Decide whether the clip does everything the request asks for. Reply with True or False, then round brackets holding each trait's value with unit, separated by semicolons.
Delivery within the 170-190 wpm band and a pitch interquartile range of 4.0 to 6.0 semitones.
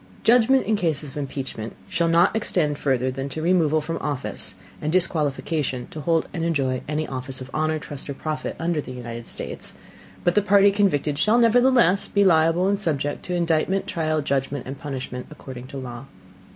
True (180 wpm; 4.6 semitones)